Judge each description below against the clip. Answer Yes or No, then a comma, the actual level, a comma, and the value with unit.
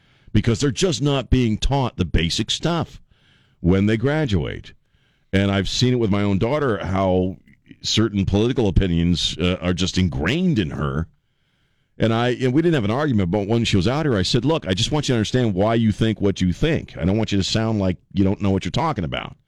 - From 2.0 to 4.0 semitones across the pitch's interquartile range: No, average, 5.3 semitones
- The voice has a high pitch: No, low, 110 Hz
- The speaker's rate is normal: No, fast, 225 wpm